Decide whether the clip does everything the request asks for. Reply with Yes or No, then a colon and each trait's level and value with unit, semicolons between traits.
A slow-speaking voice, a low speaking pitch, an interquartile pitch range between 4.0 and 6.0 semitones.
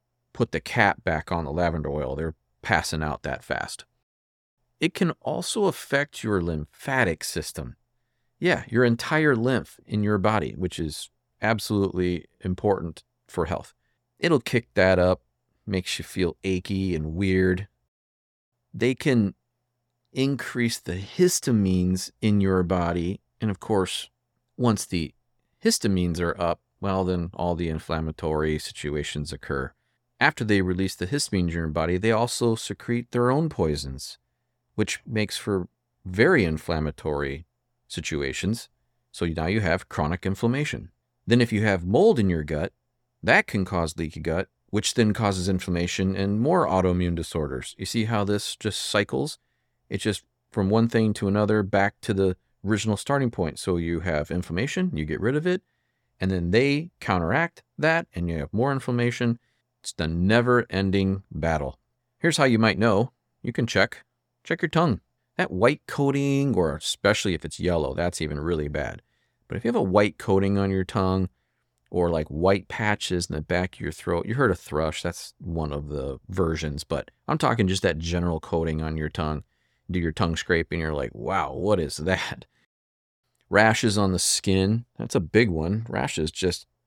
No: average, 165 wpm; very low, 95 Hz; wide, 5.4 semitones